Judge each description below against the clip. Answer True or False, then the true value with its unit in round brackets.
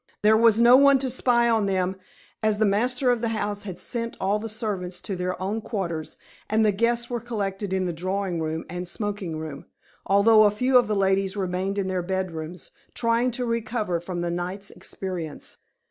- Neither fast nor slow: True (195 wpm)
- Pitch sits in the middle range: False (200 Hz)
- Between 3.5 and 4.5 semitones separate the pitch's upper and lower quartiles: True (3.9 semitones)